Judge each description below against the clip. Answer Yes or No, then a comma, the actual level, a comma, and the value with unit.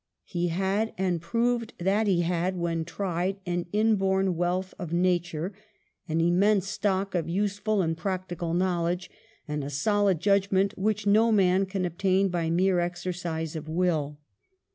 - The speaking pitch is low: No, medium, 185 Hz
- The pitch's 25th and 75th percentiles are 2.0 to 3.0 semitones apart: Yes, narrow, 2.4 semitones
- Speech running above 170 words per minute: No, average, 140 wpm